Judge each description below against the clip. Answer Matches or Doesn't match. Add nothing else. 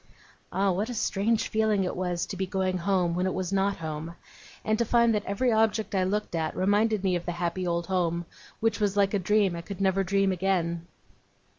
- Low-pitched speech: Doesn't match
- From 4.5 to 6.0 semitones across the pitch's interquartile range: Doesn't match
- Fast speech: Matches